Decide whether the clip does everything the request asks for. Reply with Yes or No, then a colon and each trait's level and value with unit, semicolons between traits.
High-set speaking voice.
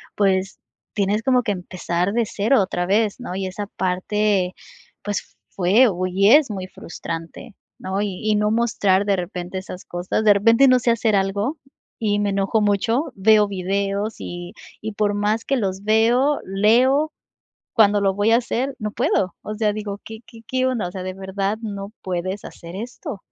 Yes: high, 205 Hz